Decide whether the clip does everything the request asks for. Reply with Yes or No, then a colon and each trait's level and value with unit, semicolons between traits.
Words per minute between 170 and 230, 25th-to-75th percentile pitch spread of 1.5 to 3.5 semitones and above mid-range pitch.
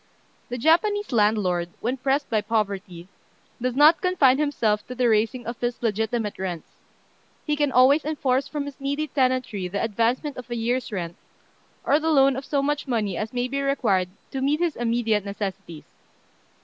No: average, 175 wpm; average, 4.8 semitones; high, 245 Hz